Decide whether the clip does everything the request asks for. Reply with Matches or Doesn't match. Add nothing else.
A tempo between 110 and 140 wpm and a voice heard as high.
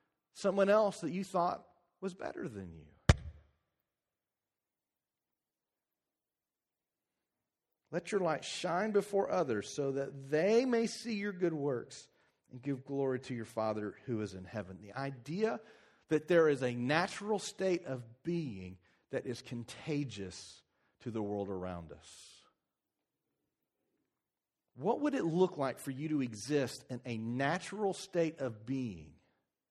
Doesn't match